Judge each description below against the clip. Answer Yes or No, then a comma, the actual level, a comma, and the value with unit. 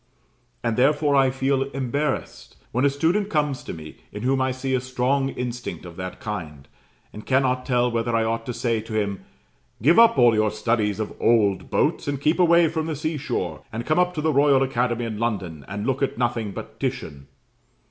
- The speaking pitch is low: Yes, low, 125 Hz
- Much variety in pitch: No, average, 4.1 semitones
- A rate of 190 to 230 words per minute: Yes, fast, 205 wpm